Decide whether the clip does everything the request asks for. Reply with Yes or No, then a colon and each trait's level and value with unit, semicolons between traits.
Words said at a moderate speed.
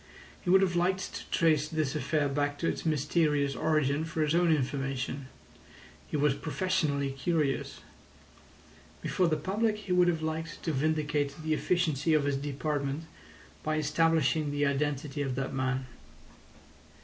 Yes: average, 150 wpm